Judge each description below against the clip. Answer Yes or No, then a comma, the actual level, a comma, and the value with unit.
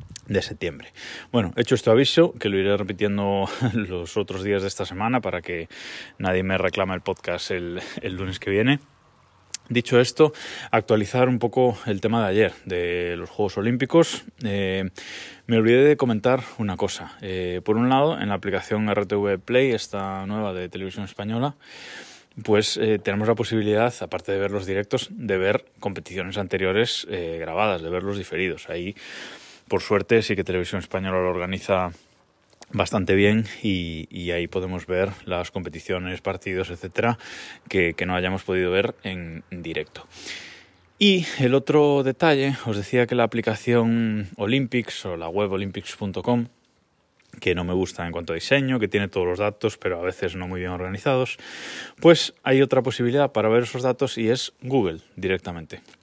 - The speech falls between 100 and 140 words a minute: No, average, 165 wpm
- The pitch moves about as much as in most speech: Yes, average, 4.5 semitones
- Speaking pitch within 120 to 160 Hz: No, low, 100 Hz